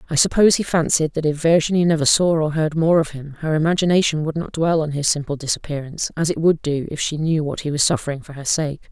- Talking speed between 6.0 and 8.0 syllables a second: Yes, 6.4 syllables/s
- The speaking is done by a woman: Yes, female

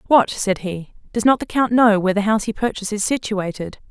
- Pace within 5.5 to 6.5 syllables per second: Yes, 6.0 syllables/s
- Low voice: No, high, 210 Hz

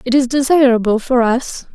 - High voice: Yes, very high, 250 Hz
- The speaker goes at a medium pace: Yes, average, 170 wpm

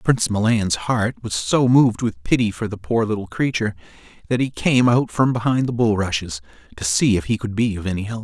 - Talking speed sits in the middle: No, fast, 220 wpm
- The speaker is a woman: No, male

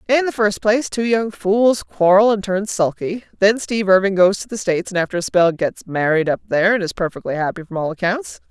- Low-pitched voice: No, high, 195 Hz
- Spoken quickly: Yes, fast, 235 wpm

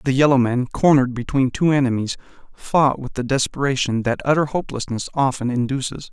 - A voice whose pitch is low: Yes, low, 130 Hz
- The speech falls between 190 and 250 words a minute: No, average, 155 wpm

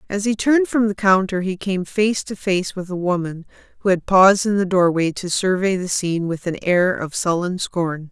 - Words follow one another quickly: Yes, fast, 220 wpm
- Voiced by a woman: Yes, female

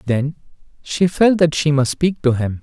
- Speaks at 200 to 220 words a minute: Yes, fast, 205 wpm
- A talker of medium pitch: Yes, medium, 150 Hz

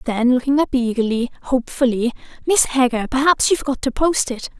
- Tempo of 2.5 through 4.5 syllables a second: No, 5.8 syllables/s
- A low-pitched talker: No, very high, 260 Hz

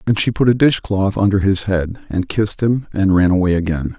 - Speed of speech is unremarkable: No, fast, 240 wpm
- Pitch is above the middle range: No, low, 100 Hz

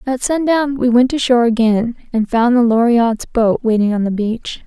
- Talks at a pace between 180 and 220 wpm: Yes, fast, 205 wpm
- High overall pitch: Yes, high, 240 Hz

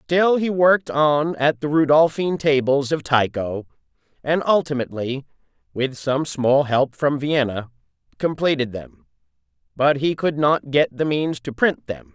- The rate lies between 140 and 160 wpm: Yes, average, 150 wpm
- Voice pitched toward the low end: No, medium, 145 Hz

